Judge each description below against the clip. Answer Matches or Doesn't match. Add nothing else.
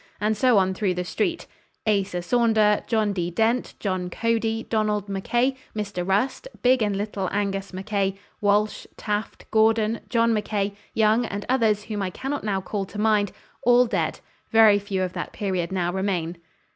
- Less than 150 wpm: Doesn't match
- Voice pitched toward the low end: Doesn't match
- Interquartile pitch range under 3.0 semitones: Matches